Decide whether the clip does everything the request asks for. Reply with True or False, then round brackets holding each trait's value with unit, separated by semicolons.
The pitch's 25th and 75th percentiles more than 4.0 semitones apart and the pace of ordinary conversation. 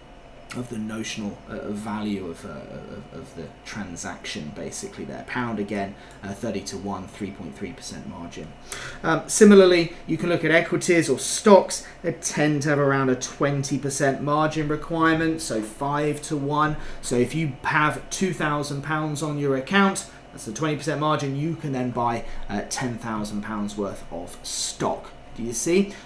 True (5.5 semitones; 175 wpm)